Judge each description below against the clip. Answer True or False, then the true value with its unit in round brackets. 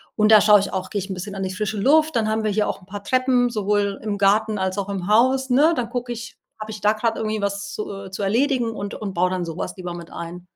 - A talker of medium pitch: False (210 Hz)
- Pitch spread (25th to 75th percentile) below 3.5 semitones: True (2.6 semitones)